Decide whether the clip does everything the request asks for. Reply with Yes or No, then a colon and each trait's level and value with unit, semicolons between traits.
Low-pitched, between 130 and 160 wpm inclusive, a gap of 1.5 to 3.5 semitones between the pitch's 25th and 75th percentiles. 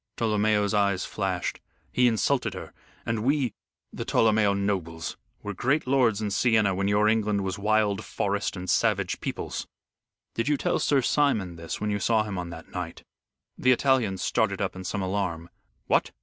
No: low, 105 Hz; average, 170 wpm; average, 2.9 semitones